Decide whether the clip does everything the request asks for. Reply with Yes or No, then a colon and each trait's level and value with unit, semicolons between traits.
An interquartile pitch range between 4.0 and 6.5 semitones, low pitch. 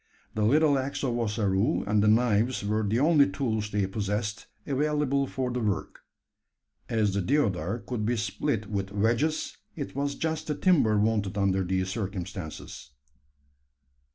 Yes: average, 5.2 semitones; low, 110 Hz